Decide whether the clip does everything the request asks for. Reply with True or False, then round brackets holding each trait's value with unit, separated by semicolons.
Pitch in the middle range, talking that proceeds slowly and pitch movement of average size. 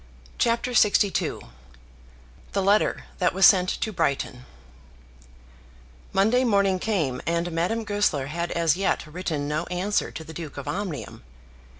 True (180 Hz; 130 wpm; 4.2 semitones)